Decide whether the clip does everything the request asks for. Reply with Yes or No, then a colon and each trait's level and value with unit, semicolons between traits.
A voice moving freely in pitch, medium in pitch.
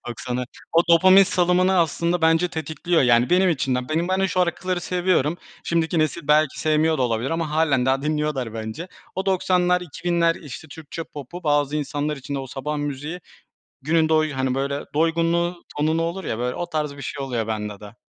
No: average, 4.0 semitones; medium, 155 Hz